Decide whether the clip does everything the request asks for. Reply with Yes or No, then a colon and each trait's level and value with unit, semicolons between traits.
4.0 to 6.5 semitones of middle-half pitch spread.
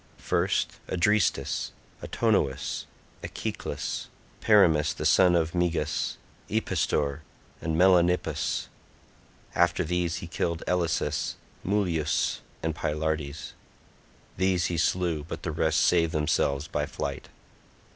No: narrow, 2.4 semitones